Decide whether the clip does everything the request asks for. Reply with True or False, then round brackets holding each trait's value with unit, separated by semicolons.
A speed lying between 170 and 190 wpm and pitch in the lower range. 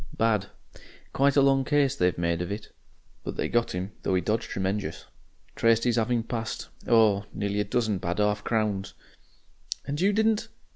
True (175 wpm; 110 Hz)